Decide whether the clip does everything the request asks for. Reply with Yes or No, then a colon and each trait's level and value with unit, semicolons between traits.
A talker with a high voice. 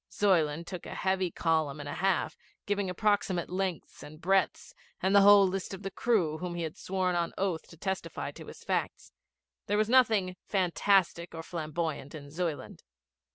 No: medium, 180 Hz